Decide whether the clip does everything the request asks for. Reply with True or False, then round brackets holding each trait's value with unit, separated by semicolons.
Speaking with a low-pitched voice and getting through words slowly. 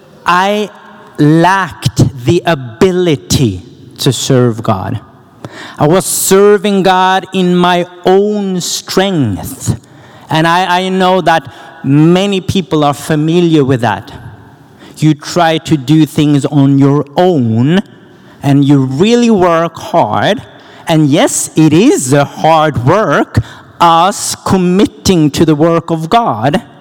False (160 Hz; 120 wpm)